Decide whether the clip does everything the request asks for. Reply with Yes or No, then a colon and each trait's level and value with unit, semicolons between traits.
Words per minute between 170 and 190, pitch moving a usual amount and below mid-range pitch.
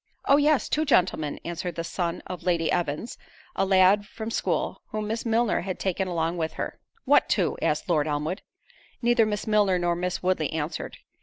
No: average, 180 wpm; average, 4.2 semitones; medium, 185 Hz